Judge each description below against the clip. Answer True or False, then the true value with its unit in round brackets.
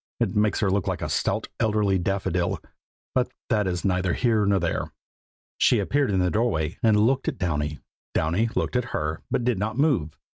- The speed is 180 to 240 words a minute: True (195 wpm)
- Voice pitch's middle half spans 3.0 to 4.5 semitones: True (4.0 semitones)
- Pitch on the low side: True (100 Hz)